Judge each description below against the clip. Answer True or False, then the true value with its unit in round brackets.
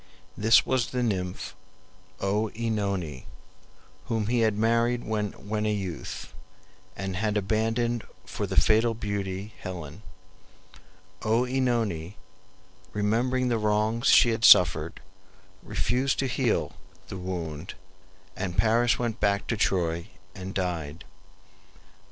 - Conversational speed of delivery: False (110 wpm)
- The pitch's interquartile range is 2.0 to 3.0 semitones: False (3.8 semitones)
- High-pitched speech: False (105 Hz)